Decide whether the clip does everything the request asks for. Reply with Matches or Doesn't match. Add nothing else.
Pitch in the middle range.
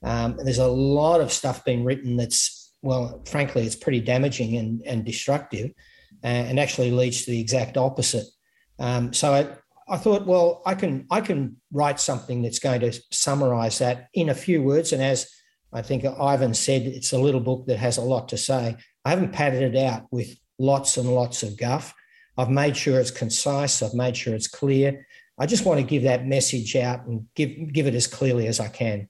Doesn't match